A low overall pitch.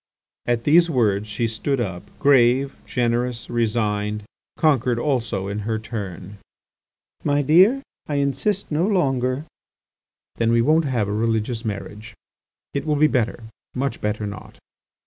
Yes: low, 120 Hz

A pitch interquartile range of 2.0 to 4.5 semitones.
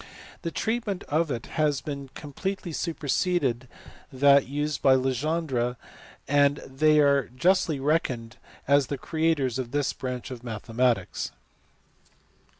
Yes: average, 3.6 semitones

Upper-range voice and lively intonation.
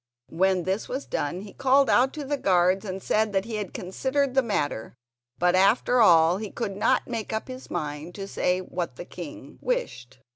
Yes: high, 195 Hz; wide, 5.8 semitones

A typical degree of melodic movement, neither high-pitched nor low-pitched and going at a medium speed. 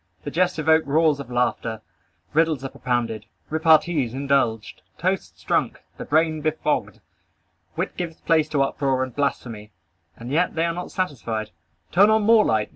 Yes: average, 5.0 semitones; medium, 145 Hz; average, 155 wpm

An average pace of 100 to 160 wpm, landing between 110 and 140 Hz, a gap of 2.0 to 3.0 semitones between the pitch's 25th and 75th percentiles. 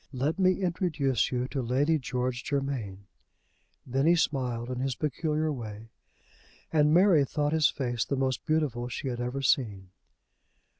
No: average, 150 wpm; low, 135 Hz; average, 3.7 semitones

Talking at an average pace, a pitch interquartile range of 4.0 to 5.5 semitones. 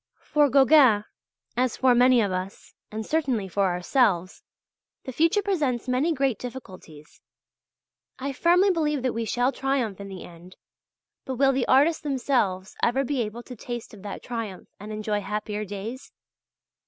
Yes: average, 155 wpm; average, 4.7 semitones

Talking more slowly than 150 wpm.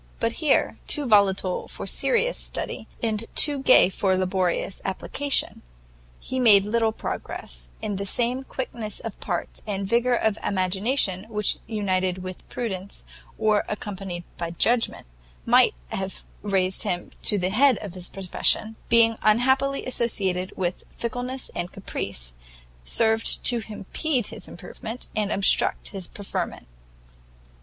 Yes: slow, 135 wpm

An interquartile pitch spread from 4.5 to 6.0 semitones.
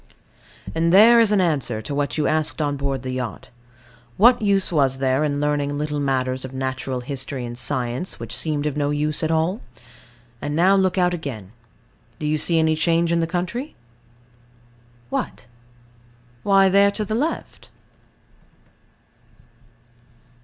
Yes: average, 5.0 semitones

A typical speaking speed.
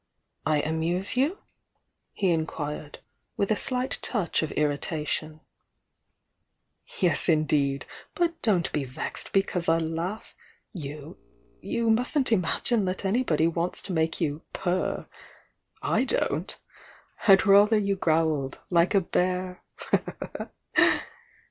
No: slow, 110 wpm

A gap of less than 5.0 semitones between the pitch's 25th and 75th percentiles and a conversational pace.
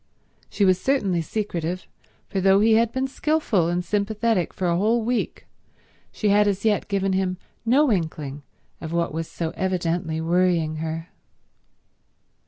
Yes: average, 4.1 semitones; average, 150 wpm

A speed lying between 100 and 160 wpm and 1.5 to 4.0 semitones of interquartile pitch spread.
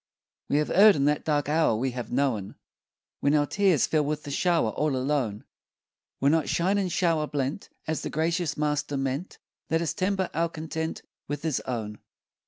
No: average, 185 wpm; average, 3.2 semitones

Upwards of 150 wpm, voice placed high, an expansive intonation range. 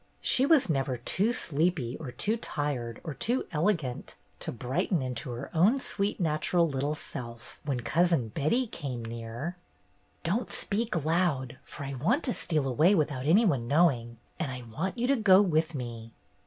No: average, 170 wpm; medium, 150 Hz; wide, 6.6 semitones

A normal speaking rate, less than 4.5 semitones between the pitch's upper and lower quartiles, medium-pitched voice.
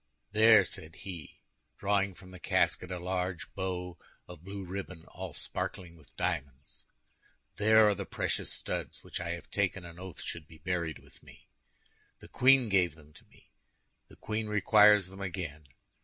No: average, 165 wpm; average, 2.8 semitones; very low, 90 Hz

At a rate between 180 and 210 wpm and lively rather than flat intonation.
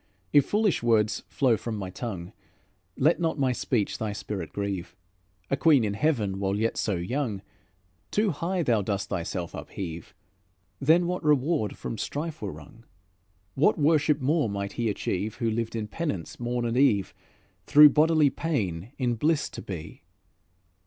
No: average, 160 wpm; wide, 6.8 semitones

